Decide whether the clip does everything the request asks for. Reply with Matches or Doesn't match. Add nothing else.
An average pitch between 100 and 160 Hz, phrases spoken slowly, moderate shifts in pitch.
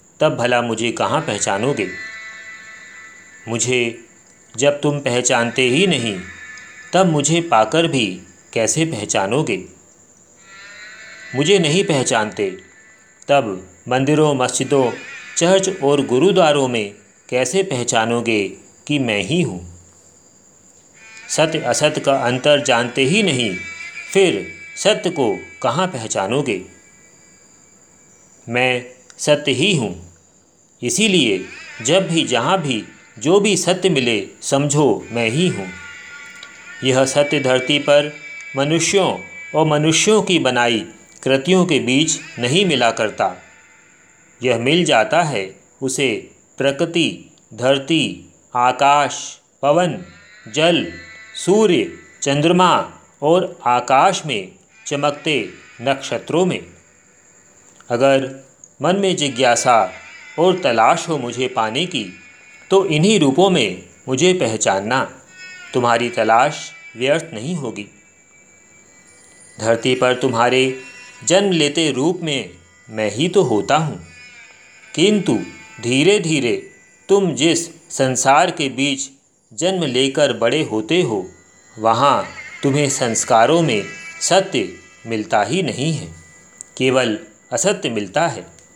Doesn't match